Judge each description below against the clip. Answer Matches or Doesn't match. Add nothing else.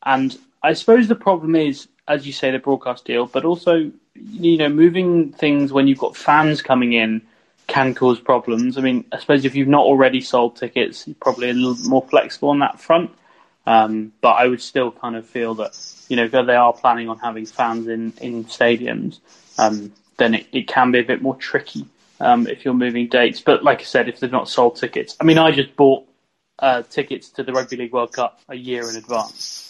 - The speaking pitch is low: Matches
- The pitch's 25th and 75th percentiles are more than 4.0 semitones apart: Doesn't match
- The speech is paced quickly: Matches